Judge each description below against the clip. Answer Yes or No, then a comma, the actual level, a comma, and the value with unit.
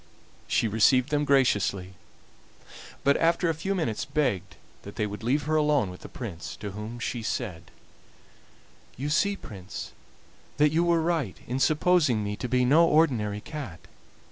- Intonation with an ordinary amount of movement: No, wide, 6.7 semitones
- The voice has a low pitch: Yes, low, 125 Hz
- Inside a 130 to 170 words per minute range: Yes, average, 160 wpm